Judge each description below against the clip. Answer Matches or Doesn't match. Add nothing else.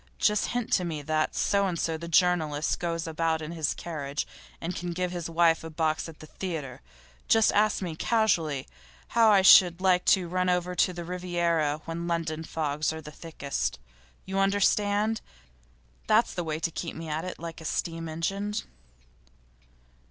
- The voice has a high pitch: Doesn't match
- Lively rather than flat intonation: Doesn't match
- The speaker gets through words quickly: Doesn't match